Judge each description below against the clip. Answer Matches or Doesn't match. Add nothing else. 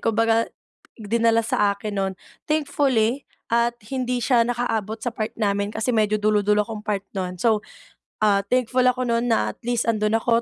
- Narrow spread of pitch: Matches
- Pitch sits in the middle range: Doesn't match